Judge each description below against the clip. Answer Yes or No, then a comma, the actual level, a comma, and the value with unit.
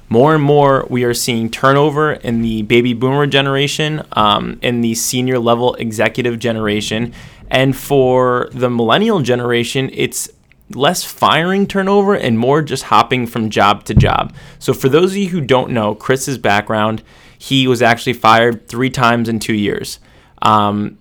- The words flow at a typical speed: Yes, average, 160 wpm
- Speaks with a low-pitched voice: Yes, low, 125 Hz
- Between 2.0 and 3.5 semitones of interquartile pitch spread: Yes, average, 3.1 semitones